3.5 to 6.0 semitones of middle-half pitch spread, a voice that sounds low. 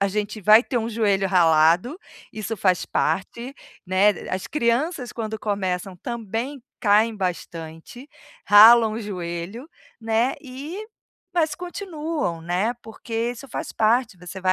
No: average, 4.6 semitones; high, 220 Hz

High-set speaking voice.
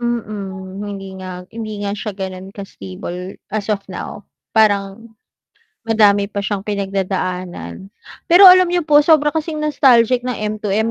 Yes: high, 205 Hz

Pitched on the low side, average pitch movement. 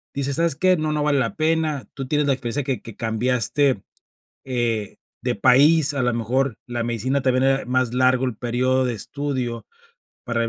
Yes: low, 130 Hz; average, 3.0 semitones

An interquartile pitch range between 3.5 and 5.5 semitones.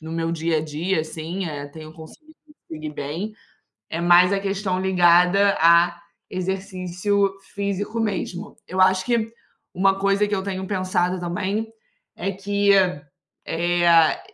No: average, 2.8 semitones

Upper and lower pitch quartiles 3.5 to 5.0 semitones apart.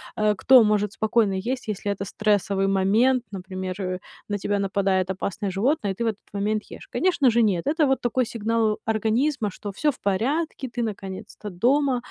Yes: average, 3.8 semitones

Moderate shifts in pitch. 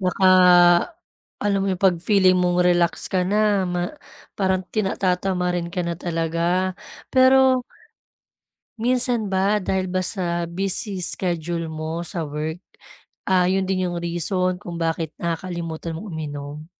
No: narrow, 2.1 semitones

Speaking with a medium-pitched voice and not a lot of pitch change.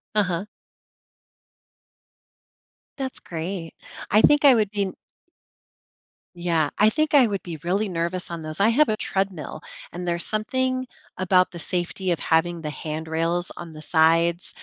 No: medium, 180 Hz; average, 4.1 semitones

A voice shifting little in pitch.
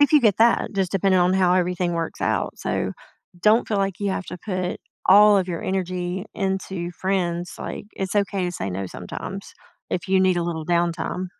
Yes: narrow, 1.9 semitones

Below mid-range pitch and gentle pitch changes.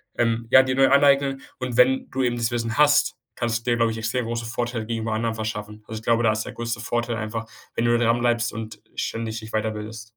Yes: low, 115 Hz; narrow, 1.3 semitones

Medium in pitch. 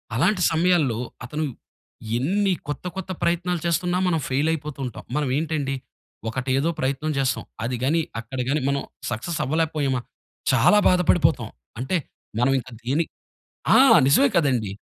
Yes: medium, 150 Hz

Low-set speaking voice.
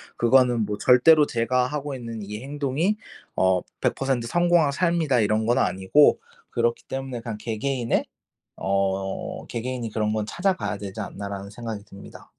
Yes: low, 120 Hz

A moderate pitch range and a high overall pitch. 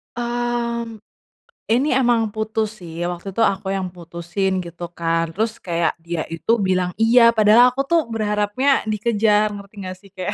Yes: average, 4.3 semitones; high, 210 Hz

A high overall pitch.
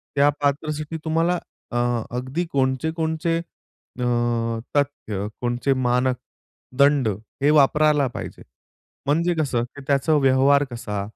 No: medium, 140 Hz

